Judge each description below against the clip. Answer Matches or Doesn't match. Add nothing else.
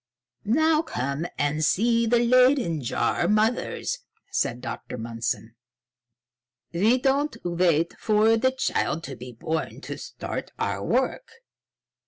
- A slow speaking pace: Matches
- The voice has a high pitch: Matches